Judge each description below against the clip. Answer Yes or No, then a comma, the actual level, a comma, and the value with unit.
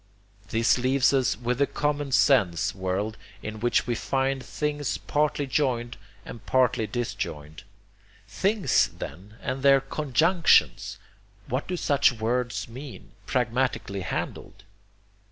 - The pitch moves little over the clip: No, average, 3.6 semitones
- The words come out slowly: Yes, slow, 120 wpm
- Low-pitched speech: Yes, low, 125 Hz